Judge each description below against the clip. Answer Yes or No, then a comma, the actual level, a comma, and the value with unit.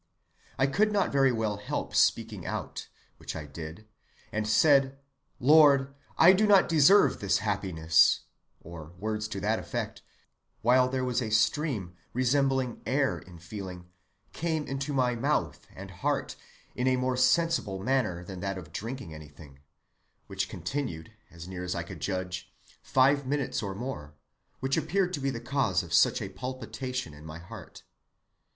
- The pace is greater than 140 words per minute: Yes, average, 160 wpm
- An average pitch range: No, wide, 7.1 semitones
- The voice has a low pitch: Yes, low, 115 Hz